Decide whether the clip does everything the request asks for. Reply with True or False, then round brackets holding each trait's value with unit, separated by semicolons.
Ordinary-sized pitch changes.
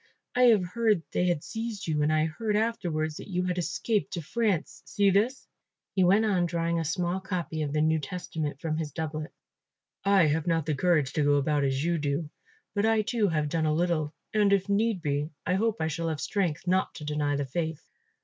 True (4.5 semitones)